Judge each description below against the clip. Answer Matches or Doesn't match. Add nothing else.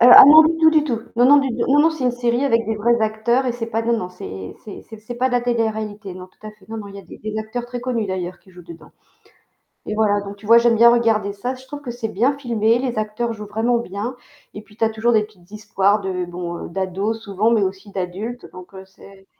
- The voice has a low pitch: Doesn't match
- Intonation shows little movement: Doesn't match